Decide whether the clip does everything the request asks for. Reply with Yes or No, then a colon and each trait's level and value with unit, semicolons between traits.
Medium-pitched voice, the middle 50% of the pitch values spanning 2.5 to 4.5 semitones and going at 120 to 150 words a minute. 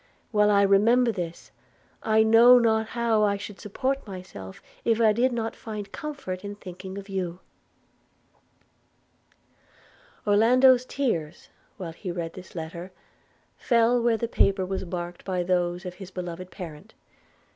No: high, 200 Hz; average, 4.0 semitones; average, 140 wpm